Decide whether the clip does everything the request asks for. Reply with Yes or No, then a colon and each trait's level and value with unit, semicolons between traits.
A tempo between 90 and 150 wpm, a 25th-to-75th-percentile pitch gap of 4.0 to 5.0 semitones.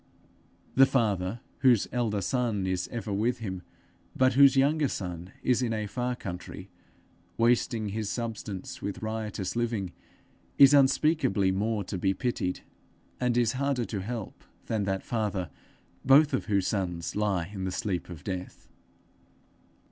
Yes: average, 140 wpm; average, 4.3 semitones